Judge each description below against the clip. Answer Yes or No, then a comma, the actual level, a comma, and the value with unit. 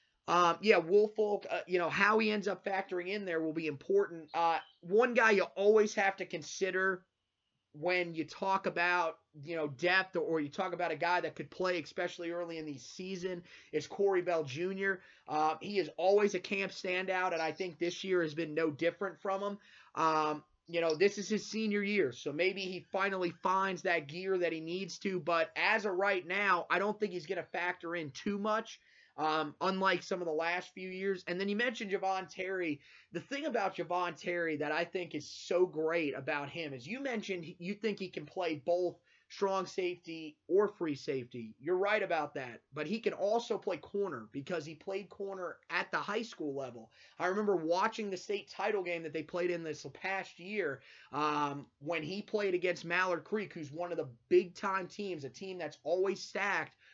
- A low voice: No, medium, 180 Hz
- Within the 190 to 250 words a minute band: Yes, fast, 205 wpm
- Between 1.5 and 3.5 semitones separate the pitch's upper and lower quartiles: Yes, average, 3.2 semitones